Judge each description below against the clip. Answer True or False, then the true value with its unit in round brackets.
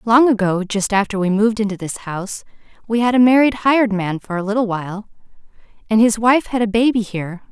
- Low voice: False (215 Hz)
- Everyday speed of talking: False (210 wpm)